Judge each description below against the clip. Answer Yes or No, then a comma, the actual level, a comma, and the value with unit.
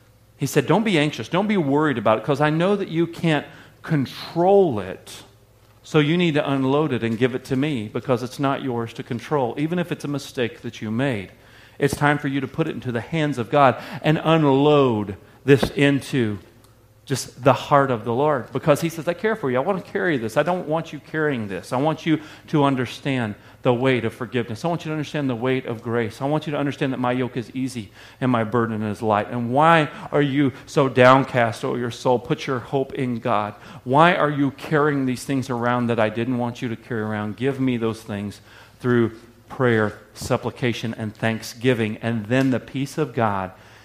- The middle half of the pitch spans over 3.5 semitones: Yes, average, 4.2 semitones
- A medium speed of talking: No, fast, 220 wpm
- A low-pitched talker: Yes, low, 130 Hz